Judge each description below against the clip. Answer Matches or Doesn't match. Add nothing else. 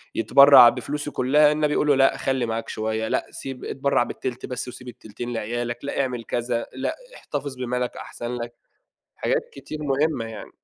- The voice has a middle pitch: Doesn't match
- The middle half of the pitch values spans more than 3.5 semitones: Doesn't match